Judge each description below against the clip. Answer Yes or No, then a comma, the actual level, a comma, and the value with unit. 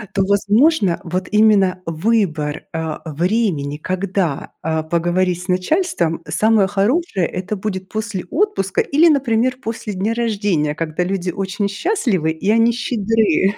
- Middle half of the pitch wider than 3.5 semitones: Yes, average, 4.3 semitones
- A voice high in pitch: Yes, high, 195 Hz